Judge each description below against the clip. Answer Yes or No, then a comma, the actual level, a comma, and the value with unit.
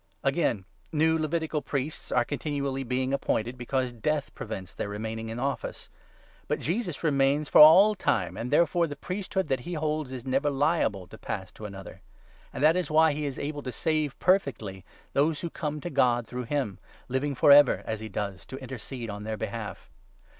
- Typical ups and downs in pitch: Yes, average, 4.9 semitones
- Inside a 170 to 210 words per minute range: Yes, average, 195 wpm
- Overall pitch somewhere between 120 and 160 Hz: Yes, low, 135 Hz